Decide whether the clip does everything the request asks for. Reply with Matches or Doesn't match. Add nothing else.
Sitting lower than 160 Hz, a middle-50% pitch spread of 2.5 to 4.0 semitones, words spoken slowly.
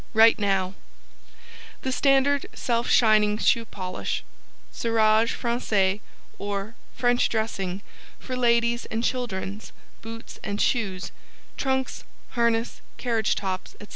Doesn't match